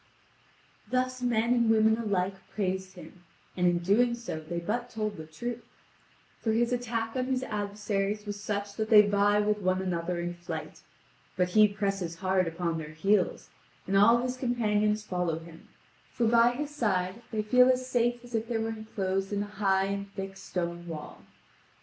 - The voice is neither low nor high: No, high, 205 Hz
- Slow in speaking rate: No, average, 180 wpm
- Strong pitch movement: No, average, 3.9 semitones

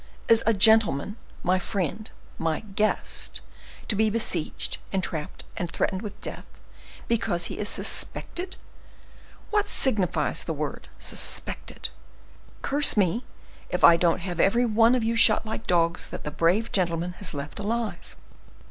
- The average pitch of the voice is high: Yes, high, 200 Hz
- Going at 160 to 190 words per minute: No, average, 140 wpm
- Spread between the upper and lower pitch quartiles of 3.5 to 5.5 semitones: Yes, average, 4.5 semitones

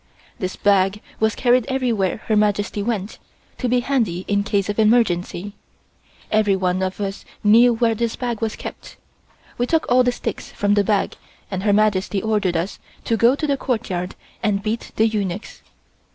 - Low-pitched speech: No, high, 210 Hz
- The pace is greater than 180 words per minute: No, average, 170 wpm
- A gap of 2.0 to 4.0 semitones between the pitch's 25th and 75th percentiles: Yes, average, 3.0 semitones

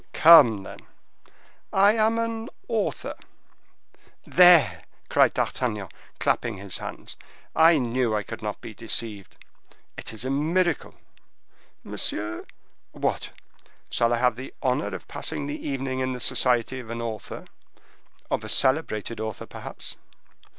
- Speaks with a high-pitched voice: No, low, 125 Hz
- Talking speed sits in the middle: No, slow, 130 wpm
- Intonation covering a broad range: Yes, wide, 6.4 semitones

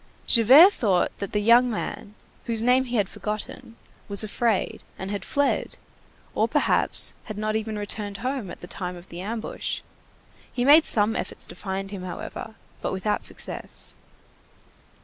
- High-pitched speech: Yes, high, 215 Hz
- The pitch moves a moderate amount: Yes, average, 3.0 semitones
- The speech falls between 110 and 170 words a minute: Yes, average, 160 wpm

